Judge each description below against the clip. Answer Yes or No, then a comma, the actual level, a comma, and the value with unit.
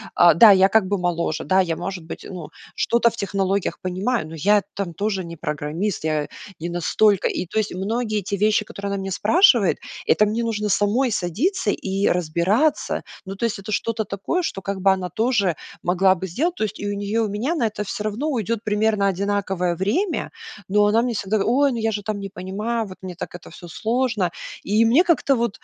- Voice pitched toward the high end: Yes, high, 200 Hz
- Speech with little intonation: No, average, 3.1 semitones